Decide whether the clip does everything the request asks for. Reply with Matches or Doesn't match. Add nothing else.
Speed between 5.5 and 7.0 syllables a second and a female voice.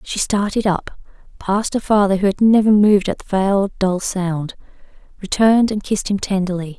Matches